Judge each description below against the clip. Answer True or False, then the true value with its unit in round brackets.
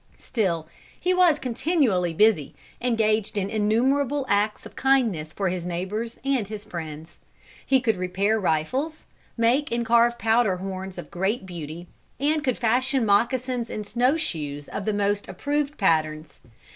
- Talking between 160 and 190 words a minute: False (145 wpm)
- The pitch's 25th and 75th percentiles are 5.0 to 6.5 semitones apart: True (5.6 semitones)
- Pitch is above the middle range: True (215 Hz)